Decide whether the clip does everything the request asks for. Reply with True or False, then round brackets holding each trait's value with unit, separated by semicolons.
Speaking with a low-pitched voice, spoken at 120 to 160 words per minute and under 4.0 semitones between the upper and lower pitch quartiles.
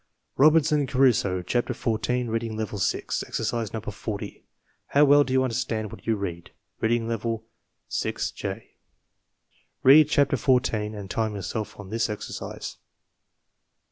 True (115 Hz; 135 wpm; 3.4 semitones)